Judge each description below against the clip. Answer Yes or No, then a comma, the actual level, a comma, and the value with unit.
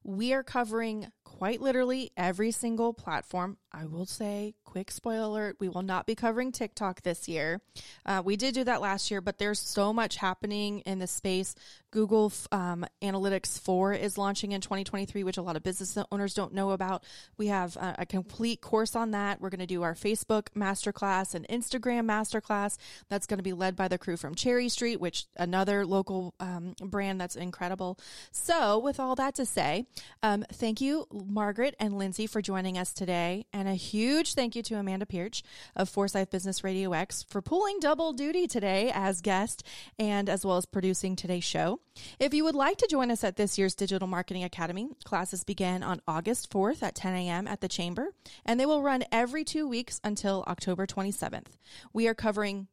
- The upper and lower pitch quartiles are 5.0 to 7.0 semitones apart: No, average, 3.2 semitones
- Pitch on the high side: Yes, high, 200 Hz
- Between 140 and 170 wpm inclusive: No, average, 195 wpm